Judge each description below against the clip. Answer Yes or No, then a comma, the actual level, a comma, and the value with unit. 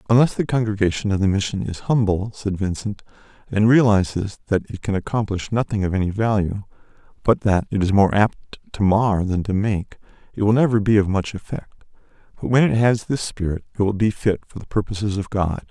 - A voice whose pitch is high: No, low, 105 Hz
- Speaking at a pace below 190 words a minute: No, average, 200 wpm